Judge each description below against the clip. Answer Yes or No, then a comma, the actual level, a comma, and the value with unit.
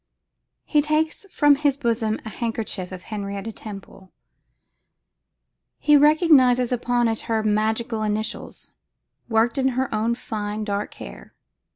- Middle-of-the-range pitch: No, high, 225 Hz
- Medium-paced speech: No, slow, 120 wpm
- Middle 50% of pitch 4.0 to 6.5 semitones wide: No, average, 3.5 semitones